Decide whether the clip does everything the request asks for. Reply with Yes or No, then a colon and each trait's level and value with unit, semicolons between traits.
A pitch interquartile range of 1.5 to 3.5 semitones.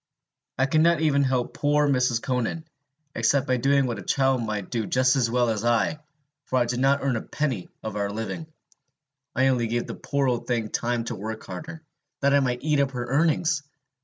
Yes: average, 3.1 semitones